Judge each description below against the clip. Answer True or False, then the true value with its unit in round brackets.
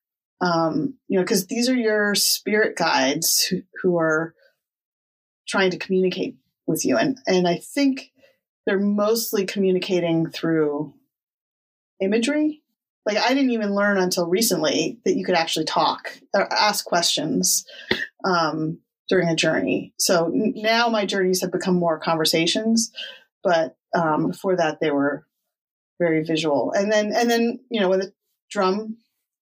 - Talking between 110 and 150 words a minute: True (145 wpm)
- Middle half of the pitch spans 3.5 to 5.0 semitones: True (4.7 semitones)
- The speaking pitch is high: True (195 Hz)